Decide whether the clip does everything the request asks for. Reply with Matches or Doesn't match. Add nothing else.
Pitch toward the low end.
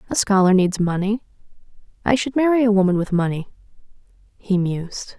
Doesn't match